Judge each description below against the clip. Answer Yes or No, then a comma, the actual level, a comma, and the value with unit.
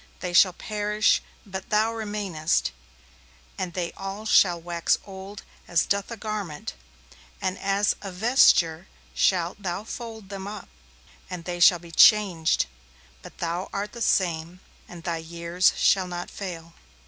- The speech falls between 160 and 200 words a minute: No, average, 145 wpm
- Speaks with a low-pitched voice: No, medium, 185 Hz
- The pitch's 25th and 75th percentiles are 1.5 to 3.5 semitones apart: Yes, average, 3.1 semitones